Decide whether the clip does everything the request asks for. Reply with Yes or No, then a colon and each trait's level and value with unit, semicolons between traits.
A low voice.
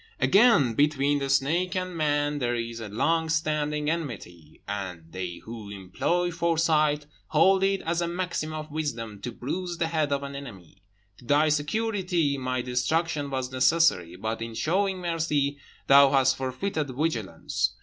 No: medium, 145 Hz